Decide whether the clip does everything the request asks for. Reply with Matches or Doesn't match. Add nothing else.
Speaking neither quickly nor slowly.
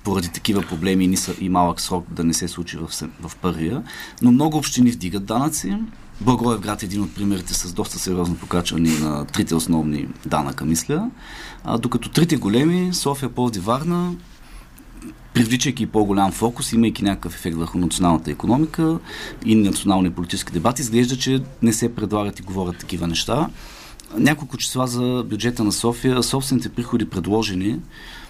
Matches